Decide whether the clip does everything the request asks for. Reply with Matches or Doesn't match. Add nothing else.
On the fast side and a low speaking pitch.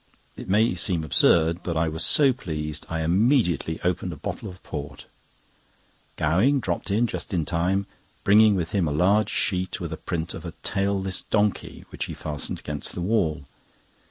Doesn't match